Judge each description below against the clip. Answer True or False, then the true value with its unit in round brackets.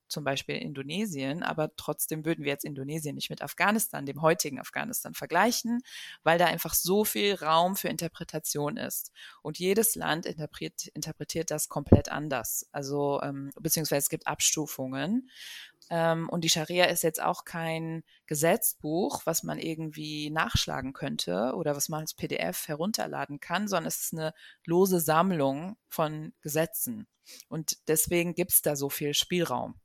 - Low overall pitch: False (160 Hz)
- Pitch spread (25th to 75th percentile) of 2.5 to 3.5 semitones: True (2.8 semitones)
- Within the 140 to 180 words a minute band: True (155 wpm)